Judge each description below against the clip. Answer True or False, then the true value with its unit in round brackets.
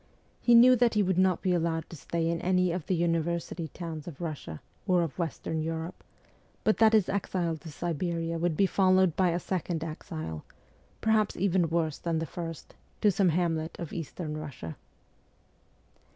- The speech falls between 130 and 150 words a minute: False (175 wpm)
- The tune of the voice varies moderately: False (2.3 semitones)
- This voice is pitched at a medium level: True (170 Hz)